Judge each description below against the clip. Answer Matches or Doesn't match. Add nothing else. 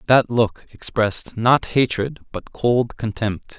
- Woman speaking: Doesn't match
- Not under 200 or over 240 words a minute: Doesn't match